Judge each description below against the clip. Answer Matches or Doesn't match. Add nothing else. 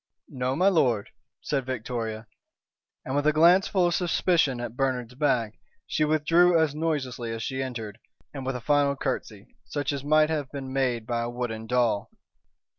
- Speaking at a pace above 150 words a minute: Matches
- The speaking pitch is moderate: Doesn't match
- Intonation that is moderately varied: Matches